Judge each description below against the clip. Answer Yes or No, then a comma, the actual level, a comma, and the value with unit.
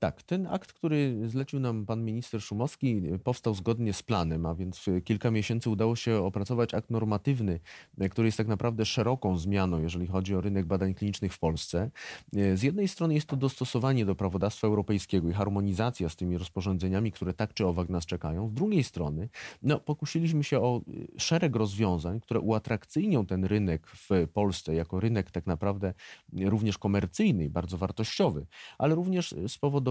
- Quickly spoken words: Yes, fast, 170 wpm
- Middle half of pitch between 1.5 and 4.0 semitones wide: No, average, 4.5 semitones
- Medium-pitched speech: No, low, 105 Hz